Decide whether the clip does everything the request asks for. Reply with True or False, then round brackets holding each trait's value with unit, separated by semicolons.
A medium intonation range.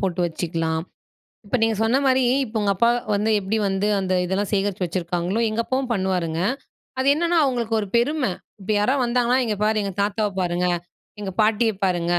True (4.2 semitones)